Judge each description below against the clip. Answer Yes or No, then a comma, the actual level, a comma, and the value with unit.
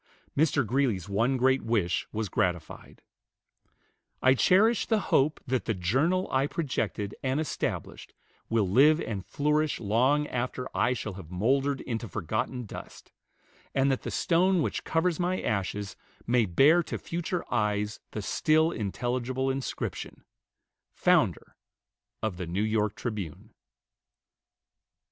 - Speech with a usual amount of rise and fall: No, wide, 5.8 semitones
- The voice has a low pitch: Yes, low, 125 Hz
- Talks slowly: Yes, slow, 130 wpm